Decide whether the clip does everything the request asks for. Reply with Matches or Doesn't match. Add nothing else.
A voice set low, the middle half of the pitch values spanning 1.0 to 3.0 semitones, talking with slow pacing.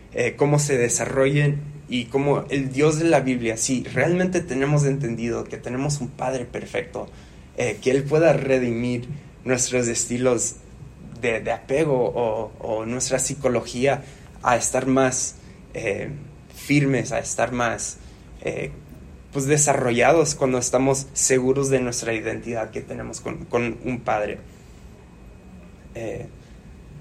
Matches